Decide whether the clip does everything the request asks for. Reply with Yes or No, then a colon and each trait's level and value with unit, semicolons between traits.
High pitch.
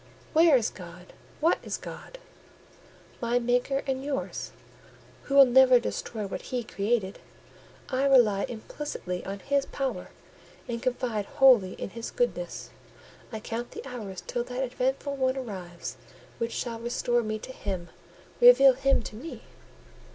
Yes: high, 245 Hz